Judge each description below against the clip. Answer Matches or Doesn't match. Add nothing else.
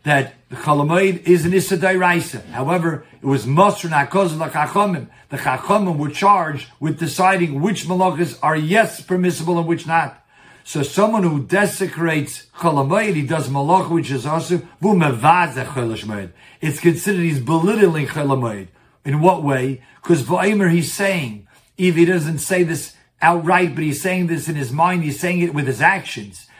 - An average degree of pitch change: Matches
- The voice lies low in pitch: Doesn't match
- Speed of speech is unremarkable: Matches